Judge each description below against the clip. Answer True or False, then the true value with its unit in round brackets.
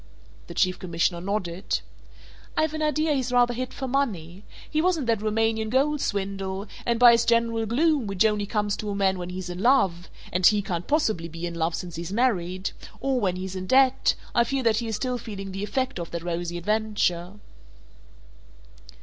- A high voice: True (210 Hz)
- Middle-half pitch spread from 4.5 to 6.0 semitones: True (5.2 semitones)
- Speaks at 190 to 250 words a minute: True (195 wpm)